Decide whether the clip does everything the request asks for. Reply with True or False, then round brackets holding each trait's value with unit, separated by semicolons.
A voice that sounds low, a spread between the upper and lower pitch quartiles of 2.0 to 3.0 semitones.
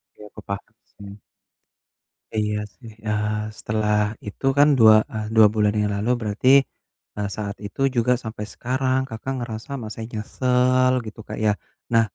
True (110 Hz; 2.7 semitones)